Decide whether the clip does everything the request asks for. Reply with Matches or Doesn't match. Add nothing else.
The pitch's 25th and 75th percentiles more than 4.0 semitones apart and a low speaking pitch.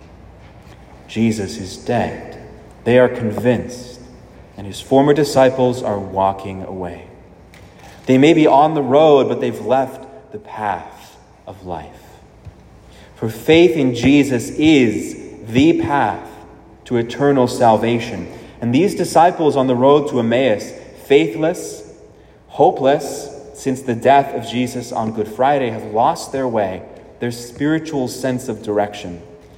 Matches